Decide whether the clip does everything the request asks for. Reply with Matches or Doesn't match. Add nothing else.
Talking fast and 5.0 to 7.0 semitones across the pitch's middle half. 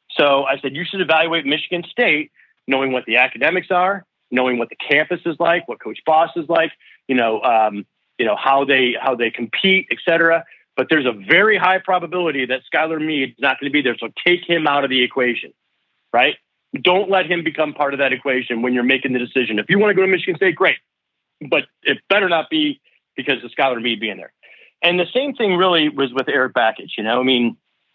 Matches